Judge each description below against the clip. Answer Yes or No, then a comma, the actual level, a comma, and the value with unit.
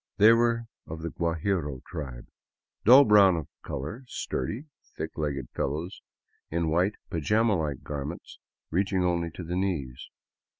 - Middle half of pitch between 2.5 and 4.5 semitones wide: No, average, 4.9 semitones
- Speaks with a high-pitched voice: No, very low, 85 Hz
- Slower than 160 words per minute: Yes, average, 145 wpm